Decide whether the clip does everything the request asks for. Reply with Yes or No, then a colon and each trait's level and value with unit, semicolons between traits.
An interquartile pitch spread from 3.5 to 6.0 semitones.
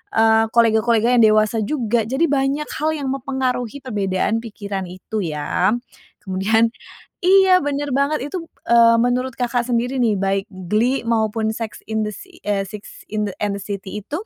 Yes: average, 3.9 semitones